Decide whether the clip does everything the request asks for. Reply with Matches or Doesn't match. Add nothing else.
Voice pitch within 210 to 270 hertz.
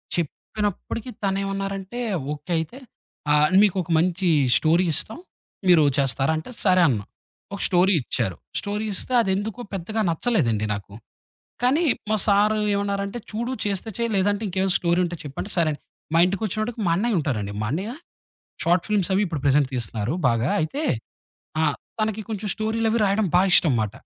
Doesn't match